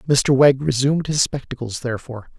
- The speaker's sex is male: Yes, male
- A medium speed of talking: Yes, average, 150 wpm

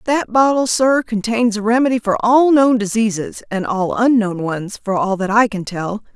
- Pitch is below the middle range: No, high, 220 Hz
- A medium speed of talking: Yes, average, 195 wpm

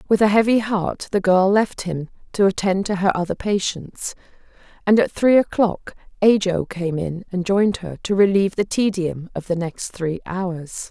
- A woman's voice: Yes, female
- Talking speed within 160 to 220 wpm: Yes, average, 180 wpm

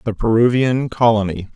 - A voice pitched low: Yes, low, 115 Hz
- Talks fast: No, slow, 115 wpm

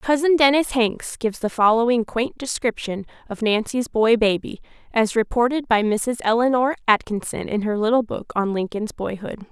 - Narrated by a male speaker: No, female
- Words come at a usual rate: Yes, average, 160 wpm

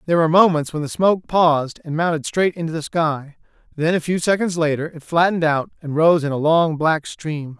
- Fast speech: Yes, fast, 220 wpm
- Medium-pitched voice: Yes, medium, 160 Hz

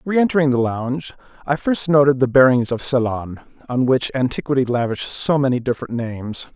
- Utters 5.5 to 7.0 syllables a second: Yes, 5.7 syllables/s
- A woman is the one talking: No, male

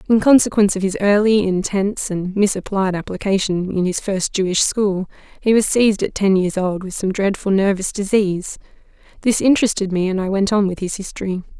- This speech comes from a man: No, female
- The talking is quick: No, average, 185 wpm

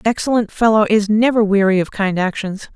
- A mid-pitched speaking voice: No, high, 210 Hz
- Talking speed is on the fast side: No, average, 195 wpm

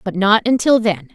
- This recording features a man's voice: No, female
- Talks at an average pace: No, fast, 210 wpm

